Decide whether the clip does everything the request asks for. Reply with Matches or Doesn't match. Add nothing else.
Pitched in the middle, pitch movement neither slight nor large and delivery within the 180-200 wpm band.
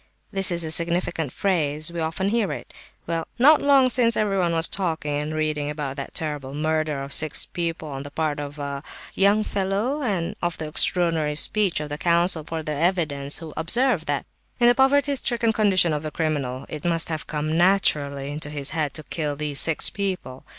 Matches